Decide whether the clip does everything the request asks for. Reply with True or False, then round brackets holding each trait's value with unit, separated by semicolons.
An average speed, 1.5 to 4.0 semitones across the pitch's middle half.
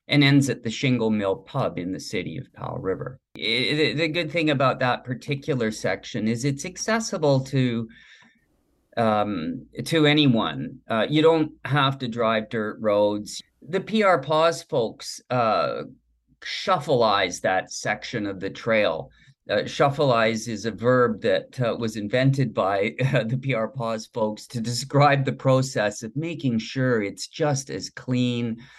False (155 wpm; 4.6 semitones)